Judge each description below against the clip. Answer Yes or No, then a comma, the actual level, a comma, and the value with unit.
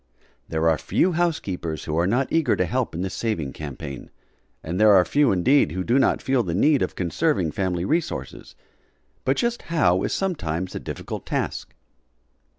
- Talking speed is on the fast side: No, average, 175 wpm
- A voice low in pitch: Yes, very low, 95 Hz